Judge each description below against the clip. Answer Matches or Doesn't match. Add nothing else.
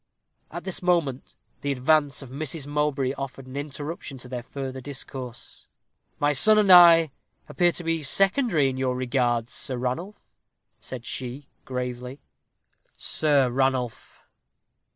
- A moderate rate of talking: Doesn't match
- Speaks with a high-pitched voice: Doesn't match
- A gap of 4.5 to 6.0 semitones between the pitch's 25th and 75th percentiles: Doesn't match